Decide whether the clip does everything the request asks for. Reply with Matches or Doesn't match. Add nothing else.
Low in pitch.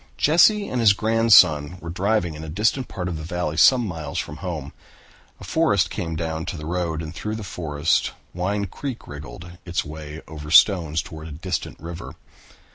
Matches